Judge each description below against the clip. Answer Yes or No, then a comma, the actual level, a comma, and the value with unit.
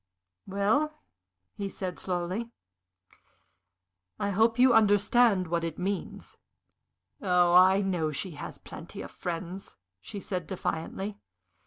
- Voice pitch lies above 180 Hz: Yes, high, 190 Hz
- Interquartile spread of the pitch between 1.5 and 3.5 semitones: Yes, narrow, 2.6 semitones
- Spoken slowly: Yes, slow, 115 wpm